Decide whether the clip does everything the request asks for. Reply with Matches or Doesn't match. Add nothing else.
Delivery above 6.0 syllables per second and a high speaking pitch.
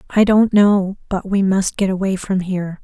Doesn't match